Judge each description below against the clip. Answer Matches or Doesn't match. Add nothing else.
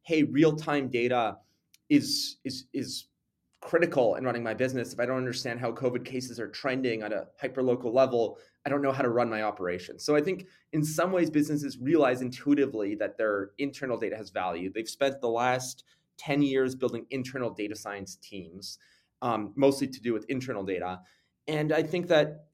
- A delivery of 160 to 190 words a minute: Matches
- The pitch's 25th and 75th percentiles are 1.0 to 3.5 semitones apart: Doesn't match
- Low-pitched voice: Matches